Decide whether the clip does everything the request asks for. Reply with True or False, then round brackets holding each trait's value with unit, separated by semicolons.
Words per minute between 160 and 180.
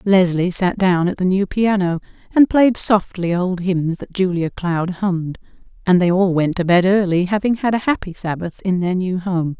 False (200 wpm)